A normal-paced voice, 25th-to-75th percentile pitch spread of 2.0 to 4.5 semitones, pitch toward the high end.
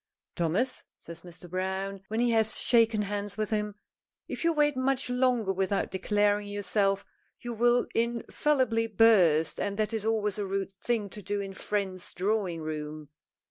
Yes: average, 165 wpm; average, 3.0 semitones; high, 205 Hz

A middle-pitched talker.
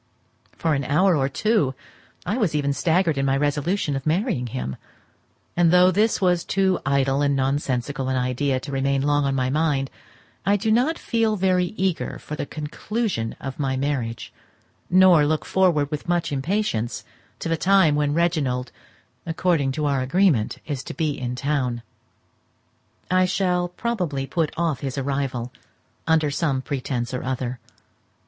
Yes: medium, 145 Hz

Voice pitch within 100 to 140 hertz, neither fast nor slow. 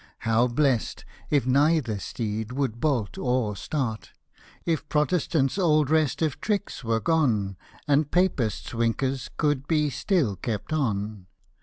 No: low, 135 Hz; slow, 130 wpm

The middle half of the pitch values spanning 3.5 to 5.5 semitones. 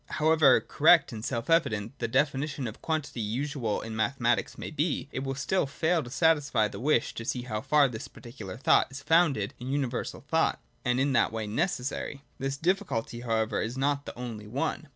Yes: average, 4.4 semitones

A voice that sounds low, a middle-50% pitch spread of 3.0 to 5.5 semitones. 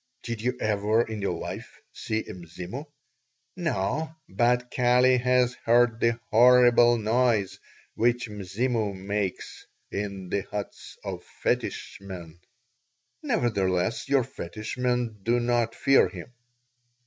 Yes: low, 115 Hz; average, 3.4 semitones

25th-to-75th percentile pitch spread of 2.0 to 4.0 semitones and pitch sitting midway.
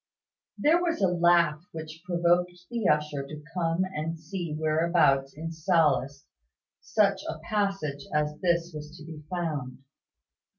Yes: average, 2.8 semitones; medium, 165 Hz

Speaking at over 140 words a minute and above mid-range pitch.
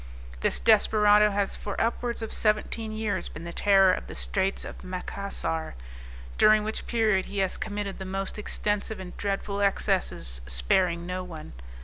Yes: average, 155 wpm; high, 200 Hz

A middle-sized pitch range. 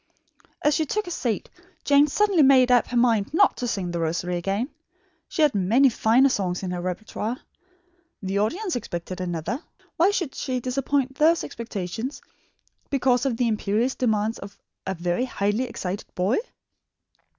No: wide, 5.7 semitones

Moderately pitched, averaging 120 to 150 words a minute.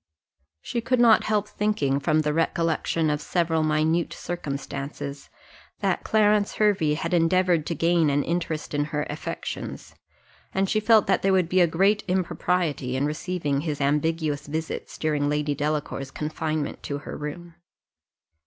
Yes: medium, 160 Hz; average, 145 wpm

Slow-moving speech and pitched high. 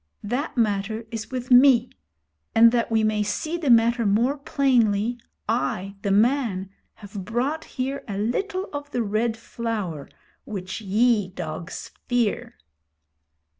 Yes: slow, 130 wpm; high, 230 Hz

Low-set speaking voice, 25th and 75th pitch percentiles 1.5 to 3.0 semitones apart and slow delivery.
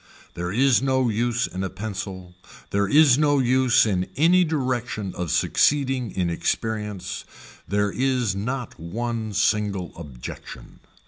No: low, 110 Hz; average, 5.1 semitones; slow, 130 wpm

